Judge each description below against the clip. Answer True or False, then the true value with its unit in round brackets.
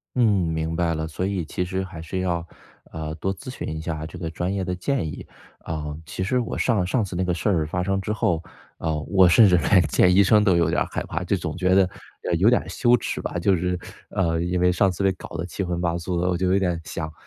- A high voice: False (90 Hz)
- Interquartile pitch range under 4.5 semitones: True (2.7 semitones)